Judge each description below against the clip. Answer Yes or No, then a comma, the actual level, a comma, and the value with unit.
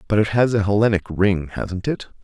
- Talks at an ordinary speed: No, fast, 215 wpm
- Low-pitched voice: Yes, low, 100 Hz